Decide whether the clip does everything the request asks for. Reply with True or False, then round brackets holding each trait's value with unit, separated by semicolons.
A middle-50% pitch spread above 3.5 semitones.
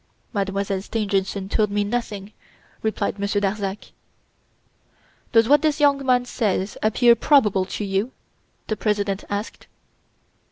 False (2.8 semitones)